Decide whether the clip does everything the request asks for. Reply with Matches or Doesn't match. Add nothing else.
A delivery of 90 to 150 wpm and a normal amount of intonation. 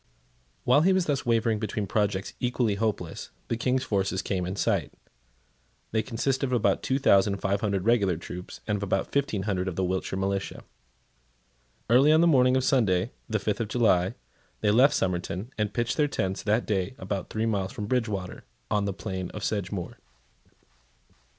Doesn't match